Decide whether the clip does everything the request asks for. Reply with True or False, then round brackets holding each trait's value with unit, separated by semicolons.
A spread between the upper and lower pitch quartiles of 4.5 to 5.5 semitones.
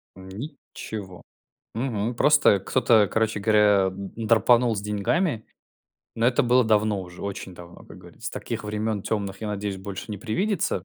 False (2.9 semitones)